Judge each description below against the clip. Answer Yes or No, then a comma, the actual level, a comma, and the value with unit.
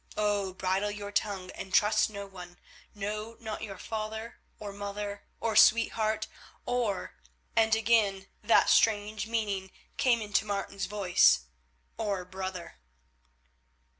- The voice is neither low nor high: No, high, 205 Hz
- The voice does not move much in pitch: Yes, narrow, 2.0 semitones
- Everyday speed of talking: No, slow, 120 wpm